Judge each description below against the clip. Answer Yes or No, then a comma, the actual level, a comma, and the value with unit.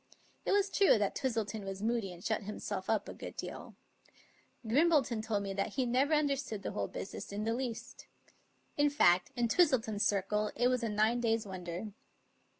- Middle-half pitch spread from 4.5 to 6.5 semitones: No, average, 4.0 semitones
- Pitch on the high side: Yes, high, 225 Hz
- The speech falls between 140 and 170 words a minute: No, average, 180 wpm